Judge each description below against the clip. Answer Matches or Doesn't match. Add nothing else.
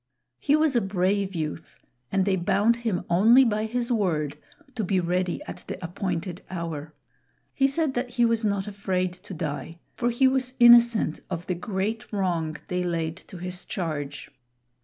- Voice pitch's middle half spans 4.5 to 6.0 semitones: Matches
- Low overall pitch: Doesn't match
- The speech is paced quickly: Doesn't match